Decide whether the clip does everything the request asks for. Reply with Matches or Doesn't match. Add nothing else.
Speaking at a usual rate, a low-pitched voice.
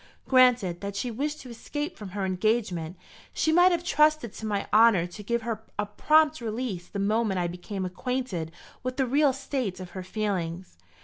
Doesn't match